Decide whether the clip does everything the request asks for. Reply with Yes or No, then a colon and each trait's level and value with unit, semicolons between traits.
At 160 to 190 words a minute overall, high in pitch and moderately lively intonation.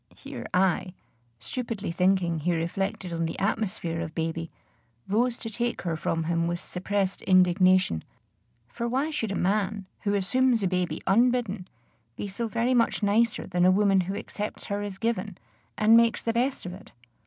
Yes: average, 170 wpm; high, 195 Hz; average, 4.1 semitones